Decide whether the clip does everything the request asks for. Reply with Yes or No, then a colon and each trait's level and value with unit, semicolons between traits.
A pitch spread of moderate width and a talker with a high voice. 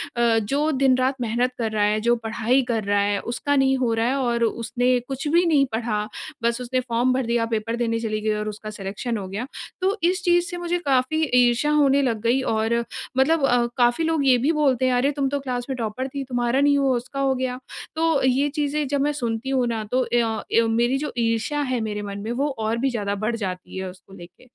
Yes: average, 3.3 semitones; high, 245 Hz